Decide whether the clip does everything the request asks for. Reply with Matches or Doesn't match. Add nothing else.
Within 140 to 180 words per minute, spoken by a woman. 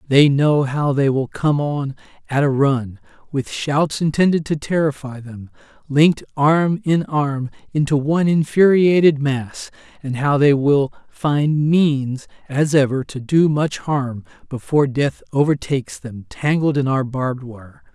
Doesn't match